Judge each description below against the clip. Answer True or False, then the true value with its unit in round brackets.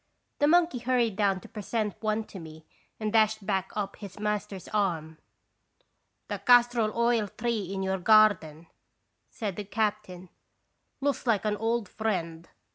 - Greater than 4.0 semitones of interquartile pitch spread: False (2.9 semitones)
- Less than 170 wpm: True (150 wpm)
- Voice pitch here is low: False (210 Hz)